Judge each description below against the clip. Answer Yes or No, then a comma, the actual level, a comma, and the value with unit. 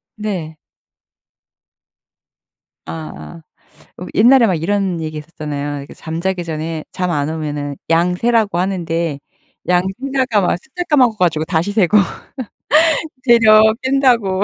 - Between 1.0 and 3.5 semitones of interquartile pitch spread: No, average, 5.2 semitones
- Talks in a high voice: No, medium, 180 Hz